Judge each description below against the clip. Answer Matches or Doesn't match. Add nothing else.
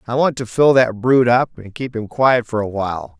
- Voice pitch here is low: Matches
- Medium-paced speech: Doesn't match